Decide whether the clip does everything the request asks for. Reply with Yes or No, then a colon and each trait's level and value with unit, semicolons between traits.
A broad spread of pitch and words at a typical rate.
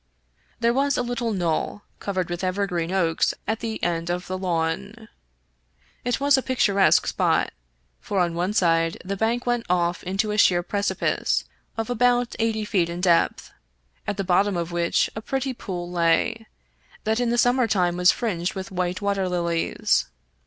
No: average, 4.5 semitones; average, 170 wpm